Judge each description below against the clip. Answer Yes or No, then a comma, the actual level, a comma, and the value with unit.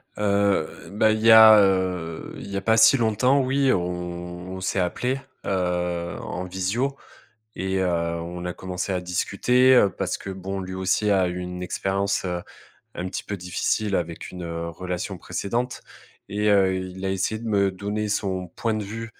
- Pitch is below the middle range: Yes, very low, 95 Hz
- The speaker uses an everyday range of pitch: Yes, average, 3.0 semitones